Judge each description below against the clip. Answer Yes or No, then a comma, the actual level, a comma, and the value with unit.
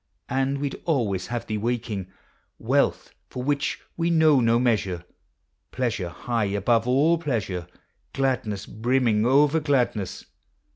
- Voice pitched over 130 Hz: No, low, 120 Hz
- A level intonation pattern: No, average, 4.4 semitones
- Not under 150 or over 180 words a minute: No, slow, 135 wpm